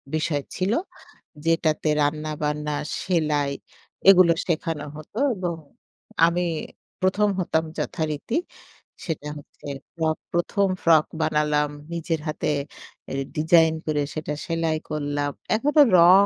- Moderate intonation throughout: No, narrow, 2.3 semitones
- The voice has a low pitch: No, medium, 160 Hz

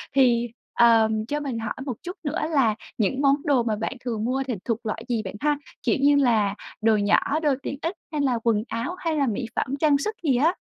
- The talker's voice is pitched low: No, very high, 250 Hz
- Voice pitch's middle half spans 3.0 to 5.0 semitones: Yes, average, 4.3 semitones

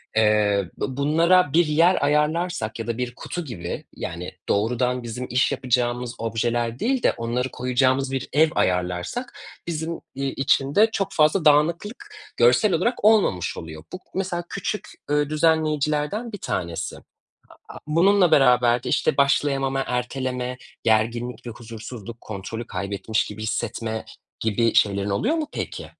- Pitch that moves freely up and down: Yes, wide, 5.8 semitones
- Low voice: Yes, low, 125 Hz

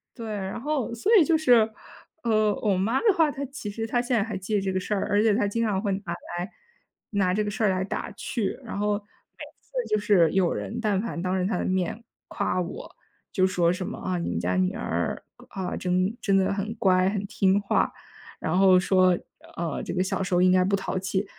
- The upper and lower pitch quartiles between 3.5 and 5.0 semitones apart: No, average, 2.8 semitones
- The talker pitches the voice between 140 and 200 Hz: Yes, high, 195 Hz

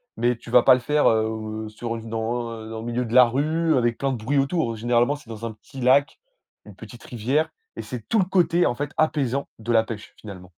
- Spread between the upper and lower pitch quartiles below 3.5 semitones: No, average, 3.8 semitones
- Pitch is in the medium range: No, low, 120 Hz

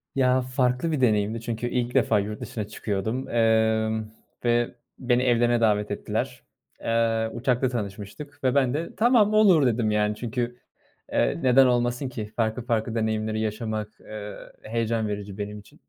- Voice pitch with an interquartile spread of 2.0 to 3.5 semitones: Yes, narrow, 2.6 semitones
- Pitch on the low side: Yes, low, 115 Hz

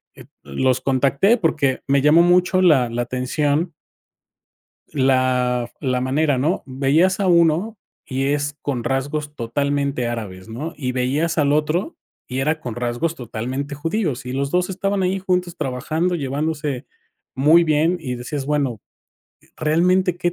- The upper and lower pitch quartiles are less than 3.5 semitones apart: No, average, 4.4 semitones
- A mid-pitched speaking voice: Yes, medium, 145 Hz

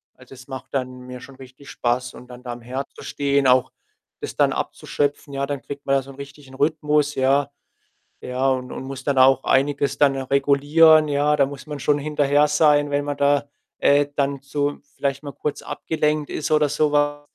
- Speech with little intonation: Yes, narrow, 1.6 semitones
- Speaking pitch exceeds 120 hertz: Yes, medium, 140 Hz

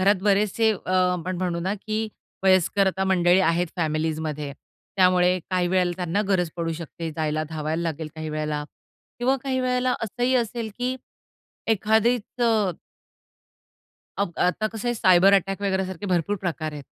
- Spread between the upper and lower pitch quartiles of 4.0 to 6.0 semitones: Yes, average, 4.3 semitones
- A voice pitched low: No, medium, 185 Hz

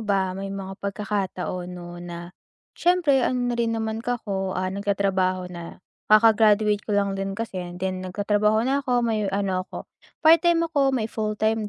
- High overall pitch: Yes, high, 205 Hz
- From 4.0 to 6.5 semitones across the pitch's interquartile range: No, average, 3.3 semitones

